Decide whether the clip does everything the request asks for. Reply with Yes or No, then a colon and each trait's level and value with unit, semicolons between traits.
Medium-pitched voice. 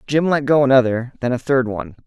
No: low, 130 Hz